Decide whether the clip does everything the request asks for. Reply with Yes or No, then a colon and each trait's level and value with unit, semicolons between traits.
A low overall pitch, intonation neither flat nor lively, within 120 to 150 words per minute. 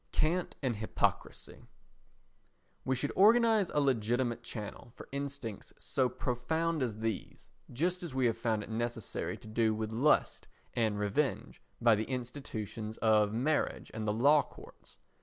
Yes: low, 120 Hz; average, 4.4 semitones; average, 145 wpm